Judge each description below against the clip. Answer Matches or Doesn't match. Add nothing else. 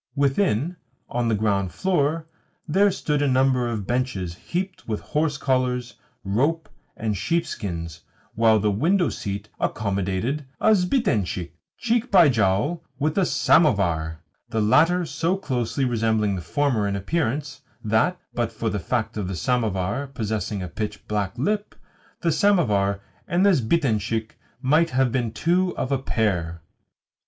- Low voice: Matches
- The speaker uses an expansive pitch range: Matches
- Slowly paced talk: Doesn't match